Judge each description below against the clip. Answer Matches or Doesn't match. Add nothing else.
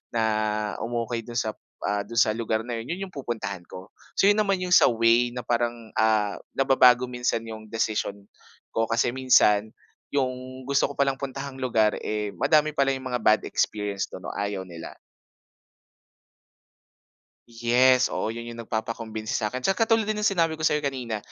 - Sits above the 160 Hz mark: Doesn't match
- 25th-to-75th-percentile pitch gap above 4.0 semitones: Doesn't match